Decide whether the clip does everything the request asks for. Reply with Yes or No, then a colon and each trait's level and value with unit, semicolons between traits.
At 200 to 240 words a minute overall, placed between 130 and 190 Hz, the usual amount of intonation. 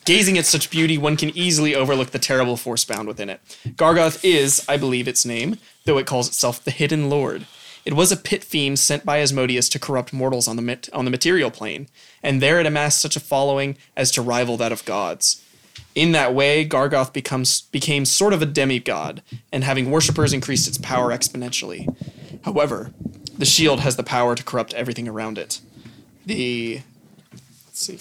No: average, 190 wpm; low, 135 Hz; average, 3.3 semitones